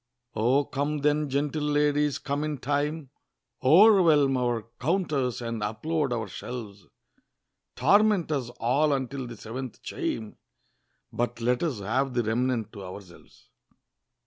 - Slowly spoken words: Yes, slow, 125 wpm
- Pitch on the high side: No, low, 135 Hz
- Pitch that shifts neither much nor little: Yes, average, 4.1 semitones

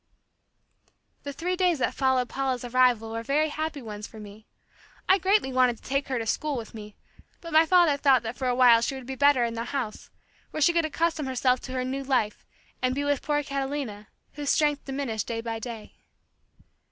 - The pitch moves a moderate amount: Yes, average, 3.8 semitones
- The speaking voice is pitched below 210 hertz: No, very high, 265 Hz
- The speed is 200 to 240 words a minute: Yes, fast, 205 wpm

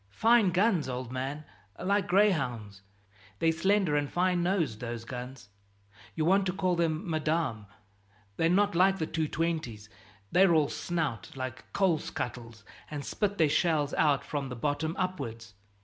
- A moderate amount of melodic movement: No, wide, 5.9 semitones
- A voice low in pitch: No, medium, 155 Hz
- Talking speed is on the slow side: No, average, 150 wpm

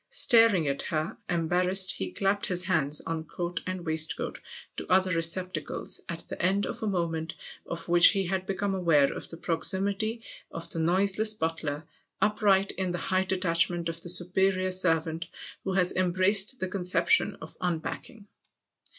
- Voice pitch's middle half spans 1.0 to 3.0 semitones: Yes, narrow, 2.5 semitones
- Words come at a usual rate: Yes, average, 160 wpm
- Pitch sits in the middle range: Yes, medium, 180 Hz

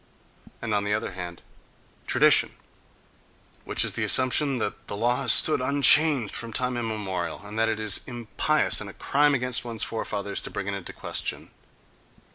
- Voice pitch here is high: No, low, 115 Hz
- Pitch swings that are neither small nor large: Yes, average, 3.8 semitones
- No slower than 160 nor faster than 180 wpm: Yes, average, 170 wpm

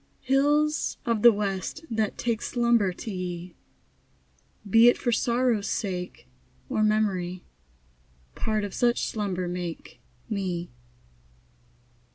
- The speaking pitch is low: No, high, 210 Hz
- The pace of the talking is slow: Yes, slow, 110 wpm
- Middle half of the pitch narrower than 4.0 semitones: No, average, 4.5 semitones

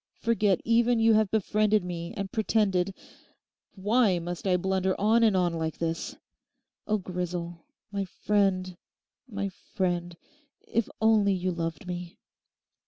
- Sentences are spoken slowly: Yes, slow, 125 wpm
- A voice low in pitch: No, high, 190 Hz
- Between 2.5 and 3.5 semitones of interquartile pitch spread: Yes, average, 3.2 semitones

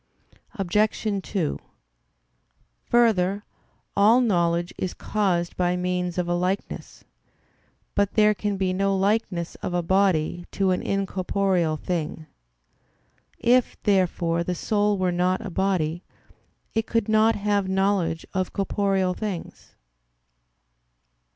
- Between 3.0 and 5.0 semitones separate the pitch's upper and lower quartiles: No, narrow, 2.5 semitones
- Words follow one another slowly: Yes, slow, 115 wpm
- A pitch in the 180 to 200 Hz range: Yes, high, 190 Hz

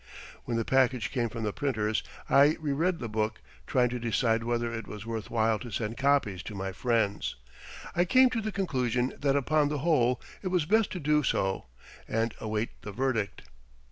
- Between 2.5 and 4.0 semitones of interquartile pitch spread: No, average, 4.5 semitones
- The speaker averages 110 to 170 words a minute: No, average, 195 wpm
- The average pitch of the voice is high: No, low, 120 Hz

